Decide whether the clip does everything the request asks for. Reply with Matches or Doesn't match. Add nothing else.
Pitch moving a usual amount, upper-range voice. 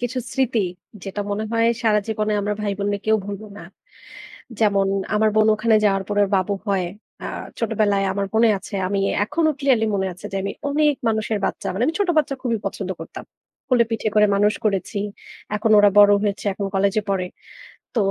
Doesn't match